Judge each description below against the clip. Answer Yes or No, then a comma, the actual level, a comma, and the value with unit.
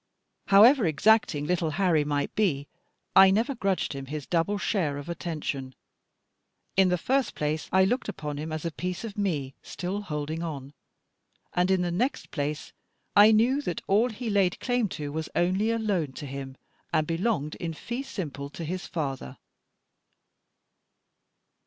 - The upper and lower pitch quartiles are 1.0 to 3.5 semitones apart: No, wide, 5.5 semitones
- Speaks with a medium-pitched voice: Yes, medium, 175 Hz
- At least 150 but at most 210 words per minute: Yes, average, 160 wpm